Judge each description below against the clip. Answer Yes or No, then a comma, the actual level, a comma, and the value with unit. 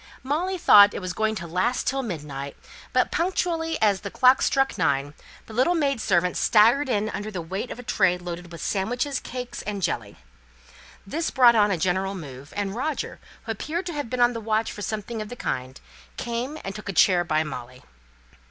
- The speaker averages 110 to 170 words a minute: No, average, 200 wpm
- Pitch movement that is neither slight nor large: No, wide, 5.9 semitones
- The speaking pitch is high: Yes, high, 210 Hz